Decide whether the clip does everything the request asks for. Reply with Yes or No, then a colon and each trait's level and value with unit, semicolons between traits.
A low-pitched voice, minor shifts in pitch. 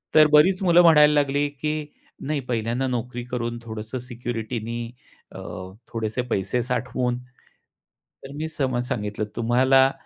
No: low, 125 Hz; average, 3.6 semitones